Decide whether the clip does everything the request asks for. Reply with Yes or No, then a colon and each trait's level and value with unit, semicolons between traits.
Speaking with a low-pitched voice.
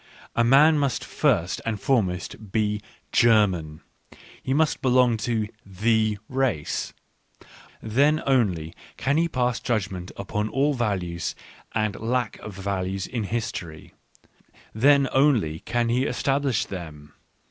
Yes: low, 110 Hz